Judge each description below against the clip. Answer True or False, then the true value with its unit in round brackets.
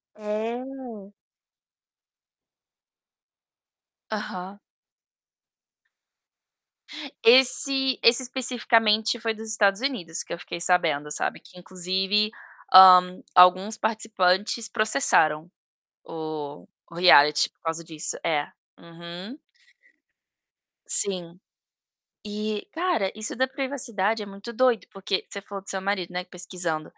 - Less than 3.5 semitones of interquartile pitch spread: False (4.1 semitones)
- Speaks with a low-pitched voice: False (200 Hz)